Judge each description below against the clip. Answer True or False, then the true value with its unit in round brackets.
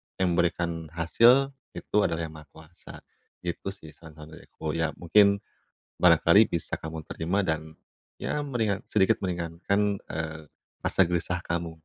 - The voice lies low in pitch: True (85 Hz)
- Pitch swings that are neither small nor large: True (3.5 semitones)